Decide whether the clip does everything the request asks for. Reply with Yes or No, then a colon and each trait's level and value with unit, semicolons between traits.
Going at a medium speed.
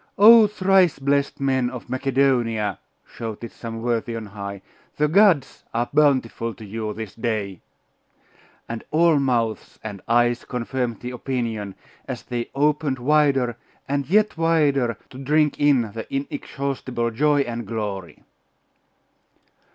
No: slow, 130 wpm